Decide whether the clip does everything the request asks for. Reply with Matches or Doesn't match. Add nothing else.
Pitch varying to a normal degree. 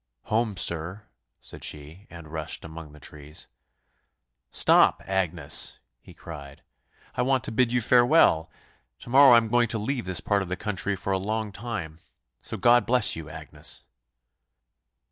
Doesn't match